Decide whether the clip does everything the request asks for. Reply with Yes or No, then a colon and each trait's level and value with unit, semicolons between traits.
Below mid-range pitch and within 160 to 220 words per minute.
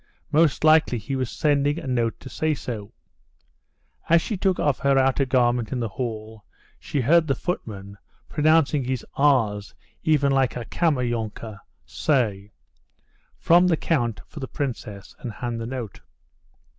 No: low, 130 Hz; average, 150 wpm